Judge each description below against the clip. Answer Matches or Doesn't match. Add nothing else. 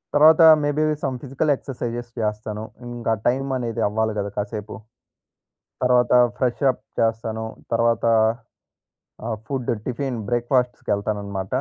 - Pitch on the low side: Matches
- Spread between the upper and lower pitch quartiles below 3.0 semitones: Matches